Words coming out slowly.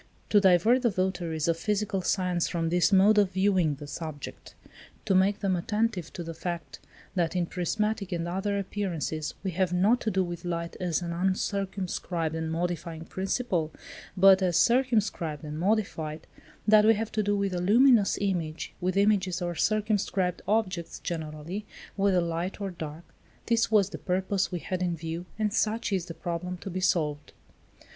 No: average, 170 wpm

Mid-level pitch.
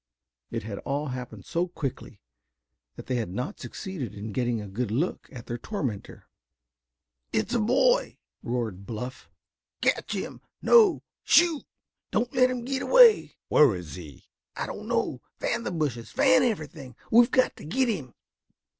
Yes: medium, 145 Hz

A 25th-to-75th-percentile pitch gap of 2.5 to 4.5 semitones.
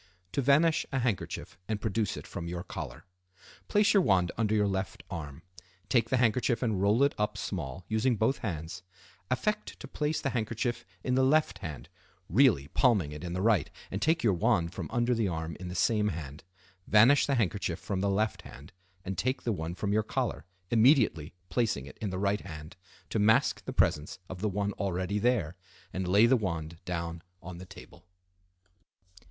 No: average, 5.2 semitones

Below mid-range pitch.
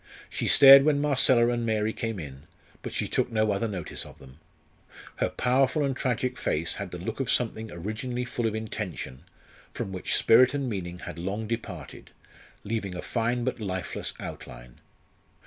Yes: low, 110 Hz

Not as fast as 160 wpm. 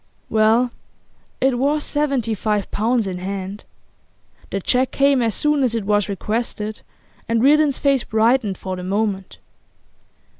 Yes: average, 140 wpm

